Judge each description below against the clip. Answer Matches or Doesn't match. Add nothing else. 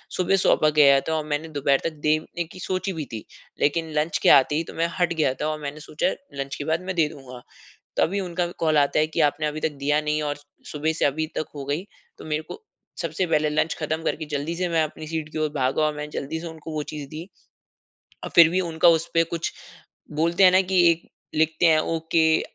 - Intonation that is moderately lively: Doesn't match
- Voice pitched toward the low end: Doesn't match